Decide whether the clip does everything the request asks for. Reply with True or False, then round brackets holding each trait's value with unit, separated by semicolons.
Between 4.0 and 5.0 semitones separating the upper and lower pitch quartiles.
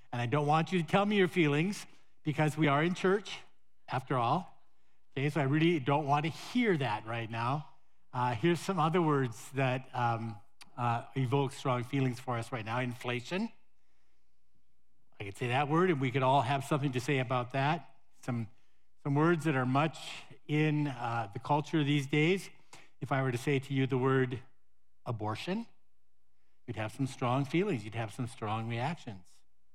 True (4.6 semitones)